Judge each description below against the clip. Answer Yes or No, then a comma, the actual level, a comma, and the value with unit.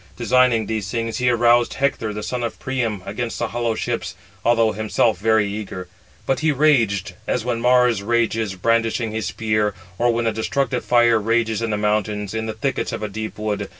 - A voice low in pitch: Yes, low, 115 Hz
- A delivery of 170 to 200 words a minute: Yes, average, 190 wpm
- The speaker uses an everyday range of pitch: No, narrow, 1.9 semitones